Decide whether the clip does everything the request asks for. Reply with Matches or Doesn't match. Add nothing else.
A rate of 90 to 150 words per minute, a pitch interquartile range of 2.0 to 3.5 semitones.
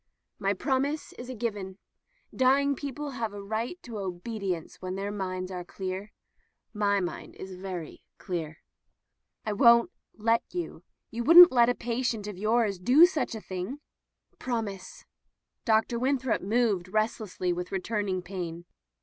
Doesn't match